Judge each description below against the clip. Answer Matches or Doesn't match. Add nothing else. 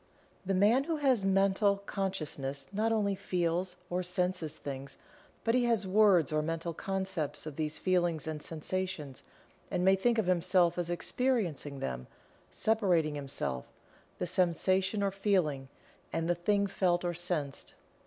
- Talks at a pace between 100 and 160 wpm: Matches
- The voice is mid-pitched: Matches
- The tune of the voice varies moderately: Matches